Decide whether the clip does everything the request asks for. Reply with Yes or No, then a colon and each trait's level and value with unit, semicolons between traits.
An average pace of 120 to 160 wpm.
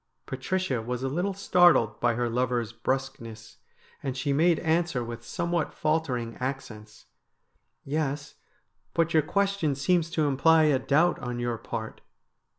Yes: average, 145 wpm